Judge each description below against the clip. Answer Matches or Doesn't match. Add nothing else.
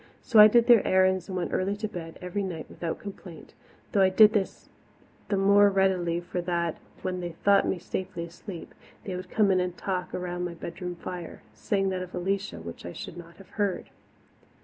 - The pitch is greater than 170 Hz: Matches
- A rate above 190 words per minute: Matches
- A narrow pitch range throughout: Matches